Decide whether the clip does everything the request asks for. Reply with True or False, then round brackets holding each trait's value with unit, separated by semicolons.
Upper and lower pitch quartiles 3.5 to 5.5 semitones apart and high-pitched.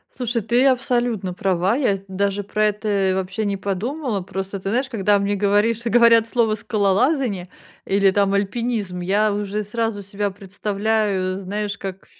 False (2.6 semitones; 205 Hz)